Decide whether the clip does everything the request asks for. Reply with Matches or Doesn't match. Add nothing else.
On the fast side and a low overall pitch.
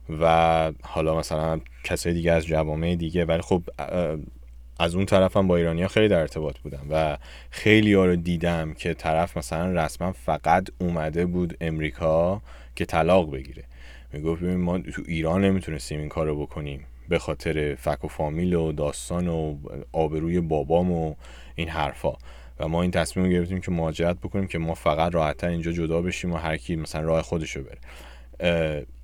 Matches